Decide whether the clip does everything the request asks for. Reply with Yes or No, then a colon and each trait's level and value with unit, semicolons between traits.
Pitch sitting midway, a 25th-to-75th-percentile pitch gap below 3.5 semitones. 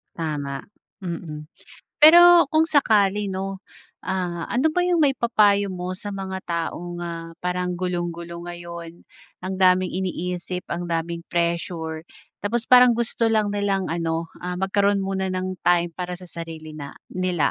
Yes: medium, 180 Hz; average, 2.9 semitones